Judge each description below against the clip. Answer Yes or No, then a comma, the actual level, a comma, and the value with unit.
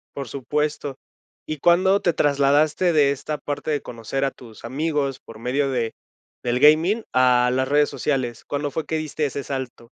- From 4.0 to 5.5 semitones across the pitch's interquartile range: No, average, 3.0 semitones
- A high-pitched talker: No, medium, 140 Hz